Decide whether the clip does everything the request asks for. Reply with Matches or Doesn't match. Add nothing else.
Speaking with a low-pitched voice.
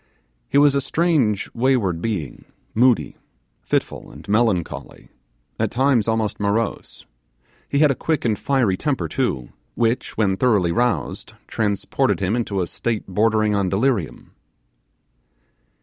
Matches